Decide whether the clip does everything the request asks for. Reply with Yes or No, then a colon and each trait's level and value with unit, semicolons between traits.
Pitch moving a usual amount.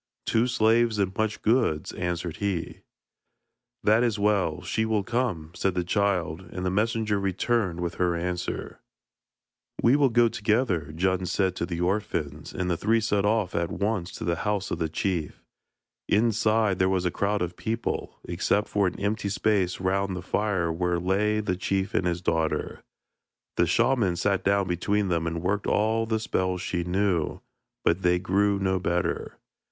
Yes: average, 3.3 semitones